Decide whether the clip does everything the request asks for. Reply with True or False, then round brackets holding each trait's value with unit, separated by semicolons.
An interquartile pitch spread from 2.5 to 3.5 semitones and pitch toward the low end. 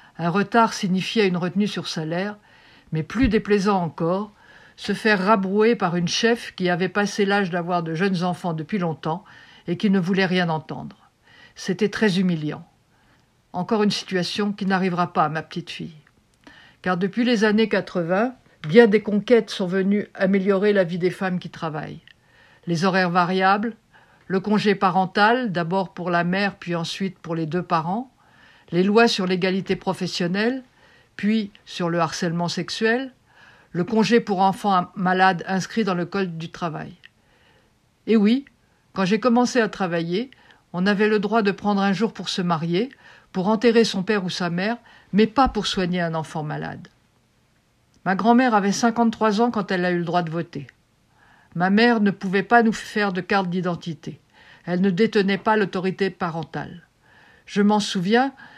False (3.2 semitones; 195 Hz)